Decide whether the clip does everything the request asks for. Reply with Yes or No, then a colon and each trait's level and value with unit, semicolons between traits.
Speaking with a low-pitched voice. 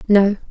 No: high, 200 Hz